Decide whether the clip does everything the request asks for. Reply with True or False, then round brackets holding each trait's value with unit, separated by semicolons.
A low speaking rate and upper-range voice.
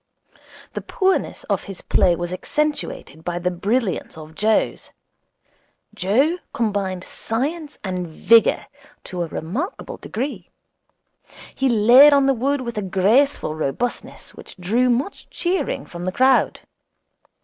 True (125 wpm; 220 Hz)